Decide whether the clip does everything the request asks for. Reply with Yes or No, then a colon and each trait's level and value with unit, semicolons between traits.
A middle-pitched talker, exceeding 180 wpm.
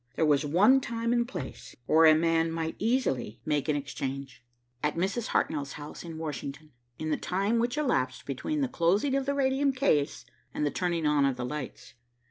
Yes: medium, 165 Hz; average, 190 wpm